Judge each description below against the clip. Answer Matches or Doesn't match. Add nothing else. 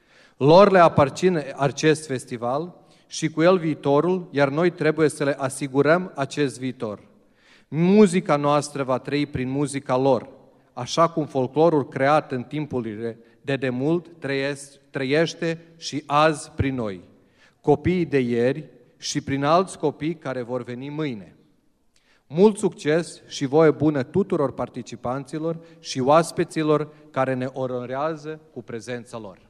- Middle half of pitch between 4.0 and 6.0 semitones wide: Doesn't match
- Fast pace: Doesn't match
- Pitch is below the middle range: Doesn't match